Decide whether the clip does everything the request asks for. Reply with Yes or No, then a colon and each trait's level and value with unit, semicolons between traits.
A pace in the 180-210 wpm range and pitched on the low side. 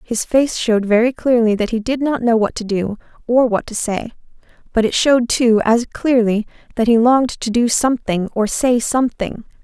No: average, 200 wpm; high, 230 Hz